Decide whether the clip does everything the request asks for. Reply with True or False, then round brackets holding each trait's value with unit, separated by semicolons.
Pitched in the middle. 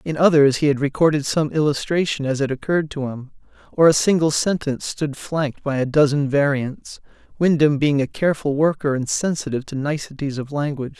True (145 Hz)